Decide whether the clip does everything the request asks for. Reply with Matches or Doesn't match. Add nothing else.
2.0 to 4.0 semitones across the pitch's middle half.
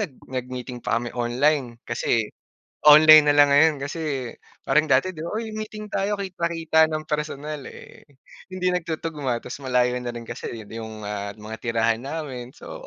Doesn't match